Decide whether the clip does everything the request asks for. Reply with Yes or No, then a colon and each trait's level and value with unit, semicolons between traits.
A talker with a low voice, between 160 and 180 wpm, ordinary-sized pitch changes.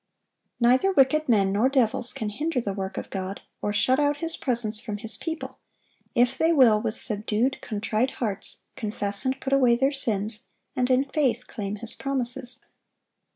No: high, 240 Hz; average, 170 wpm; average, 4.1 semitones